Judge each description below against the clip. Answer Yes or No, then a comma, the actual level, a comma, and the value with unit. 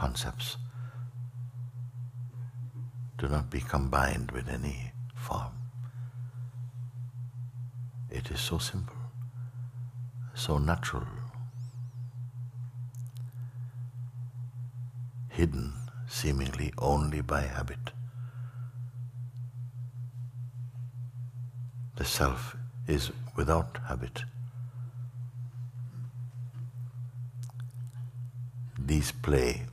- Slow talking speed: Yes, slow, 50 wpm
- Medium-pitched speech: No, low, 125 Hz